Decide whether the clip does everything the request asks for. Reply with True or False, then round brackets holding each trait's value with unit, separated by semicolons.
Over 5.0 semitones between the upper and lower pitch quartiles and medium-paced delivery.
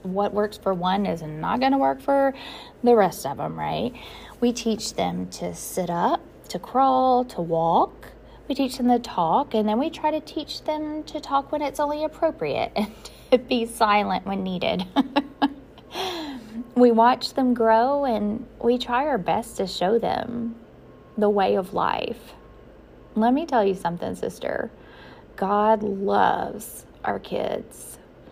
True (5.5 semitones; 160 wpm)